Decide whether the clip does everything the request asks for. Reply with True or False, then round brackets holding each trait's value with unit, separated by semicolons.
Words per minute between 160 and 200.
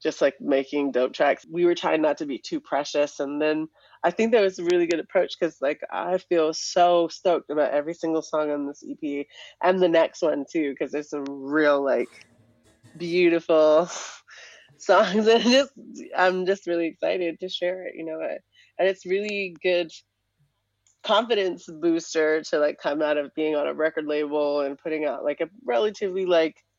True (185 wpm)